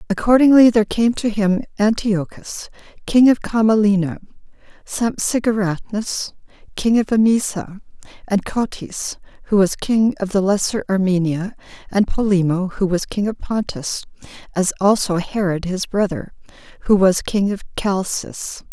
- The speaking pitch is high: Yes, high, 200 Hz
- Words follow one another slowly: Yes, slow, 125 wpm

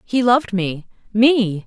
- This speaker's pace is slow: Yes, slow, 110 wpm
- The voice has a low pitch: No, high, 220 Hz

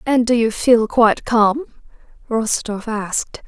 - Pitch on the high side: Yes, high, 225 Hz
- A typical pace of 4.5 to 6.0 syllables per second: No, 4.1 syllables/s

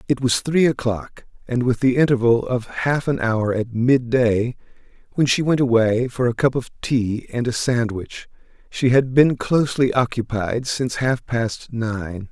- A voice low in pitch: Yes, low, 120 Hz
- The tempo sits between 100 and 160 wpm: No, average, 170 wpm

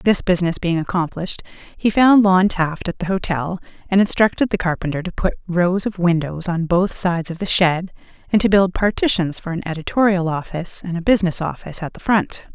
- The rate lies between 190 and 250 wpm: Yes, average, 195 wpm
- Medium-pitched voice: Yes, medium, 180 Hz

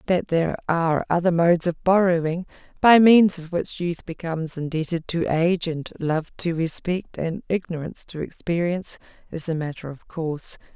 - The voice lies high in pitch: No, medium, 170 Hz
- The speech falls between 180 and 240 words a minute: No, average, 160 wpm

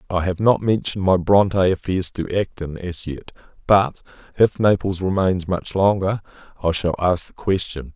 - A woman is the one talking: No, male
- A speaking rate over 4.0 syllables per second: Yes, 4.8 syllables/s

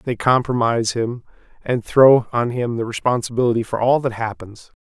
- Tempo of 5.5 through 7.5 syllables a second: No, 5.1 syllables/s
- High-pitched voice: No, low, 120 Hz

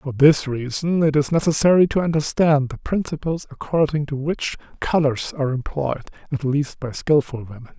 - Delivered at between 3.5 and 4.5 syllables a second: No, 5.1 syllables/s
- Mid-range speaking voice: Yes, medium, 145 Hz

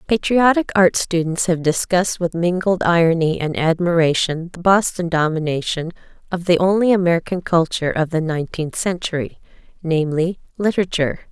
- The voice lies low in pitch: No, medium, 175 Hz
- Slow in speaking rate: Yes, slow, 125 wpm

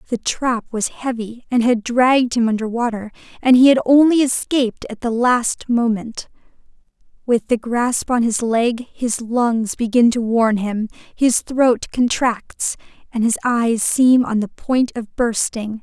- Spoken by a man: No, female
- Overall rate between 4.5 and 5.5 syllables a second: No, 4.0 syllables/s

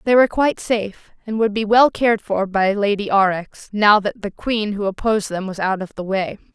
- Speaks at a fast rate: Yes, fast, 230 wpm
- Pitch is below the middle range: No, high, 205 Hz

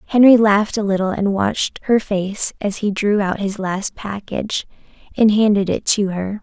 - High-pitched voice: Yes, high, 205 Hz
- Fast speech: No, average, 185 wpm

